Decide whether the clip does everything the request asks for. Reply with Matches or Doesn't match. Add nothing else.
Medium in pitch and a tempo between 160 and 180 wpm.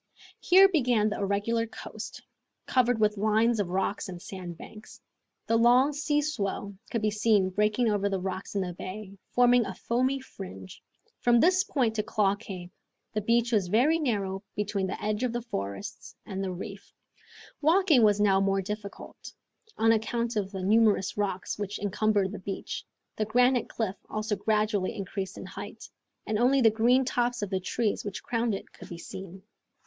Doesn't match